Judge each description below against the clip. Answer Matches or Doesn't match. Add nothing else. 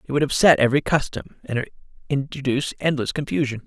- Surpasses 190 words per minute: Doesn't match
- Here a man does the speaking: Matches